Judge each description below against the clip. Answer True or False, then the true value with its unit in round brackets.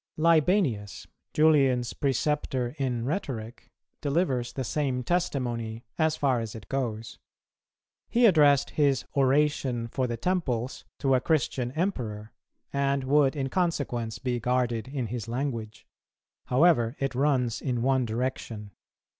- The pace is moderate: False (130 wpm)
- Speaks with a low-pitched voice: True (130 Hz)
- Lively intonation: False (3.6 semitones)